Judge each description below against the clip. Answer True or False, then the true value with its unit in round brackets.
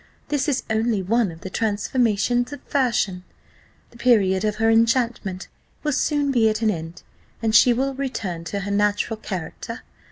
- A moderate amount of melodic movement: True (3.6 semitones)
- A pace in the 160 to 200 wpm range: True (165 wpm)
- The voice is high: True (225 Hz)